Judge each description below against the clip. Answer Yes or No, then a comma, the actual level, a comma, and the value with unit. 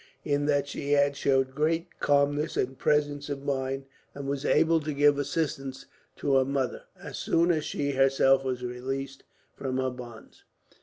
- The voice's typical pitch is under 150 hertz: Yes, medium, 140 Hz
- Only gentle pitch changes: Yes, narrow, 1.5 semitones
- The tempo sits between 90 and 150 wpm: No, average, 165 wpm